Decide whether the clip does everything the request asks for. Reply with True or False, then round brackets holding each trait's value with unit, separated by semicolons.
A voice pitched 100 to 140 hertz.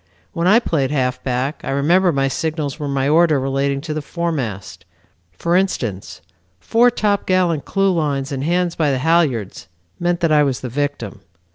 False (150 Hz)